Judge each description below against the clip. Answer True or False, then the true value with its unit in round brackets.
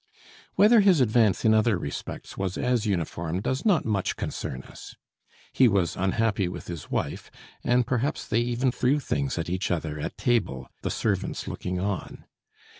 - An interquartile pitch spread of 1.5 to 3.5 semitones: False (5.5 semitones)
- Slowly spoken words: False (165 wpm)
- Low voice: True (110 Hz)